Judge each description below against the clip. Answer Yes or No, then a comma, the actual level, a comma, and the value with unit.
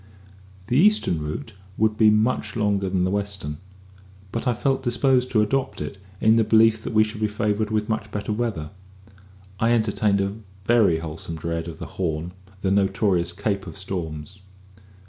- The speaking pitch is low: Yes, low, 105 Hz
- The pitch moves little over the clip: No, average, 3.3 semitones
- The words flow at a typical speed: Yes, average, 170 wpm